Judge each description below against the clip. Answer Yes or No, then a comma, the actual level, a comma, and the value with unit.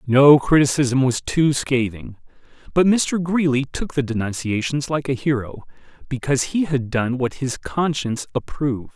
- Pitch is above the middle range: No, low, 135 Hz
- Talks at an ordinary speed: Yes, average, 145 wpm